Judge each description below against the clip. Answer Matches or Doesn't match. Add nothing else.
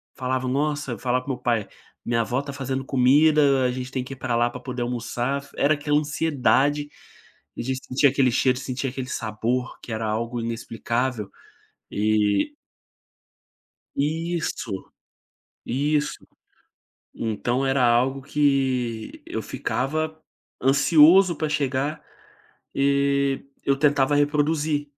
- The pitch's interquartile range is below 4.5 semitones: Matches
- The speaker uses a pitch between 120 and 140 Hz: Matches